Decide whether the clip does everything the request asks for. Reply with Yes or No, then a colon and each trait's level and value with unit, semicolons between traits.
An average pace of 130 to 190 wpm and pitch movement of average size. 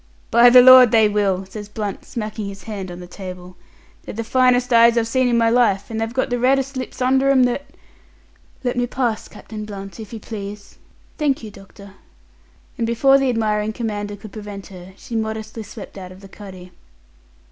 No: average, 200 wpm; average, 3.4 semitones